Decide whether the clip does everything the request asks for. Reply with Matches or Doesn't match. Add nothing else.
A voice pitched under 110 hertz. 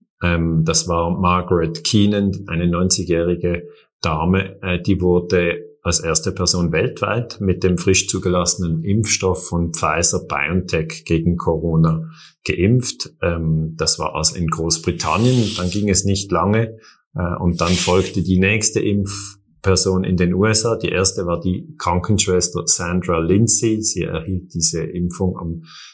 Matches